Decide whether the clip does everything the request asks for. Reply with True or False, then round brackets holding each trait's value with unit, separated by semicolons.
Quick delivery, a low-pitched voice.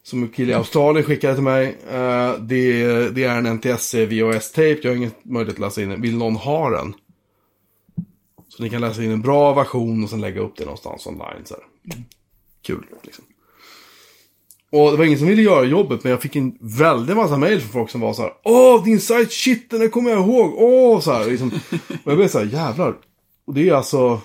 True (225 wpm; 125 Hz)